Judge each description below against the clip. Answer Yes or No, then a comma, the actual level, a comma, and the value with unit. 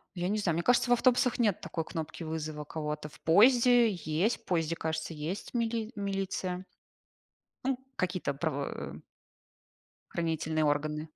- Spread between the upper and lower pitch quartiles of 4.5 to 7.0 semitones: Yes, wide, 5.5 semitones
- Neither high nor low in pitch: Yes, medium, 170 Hz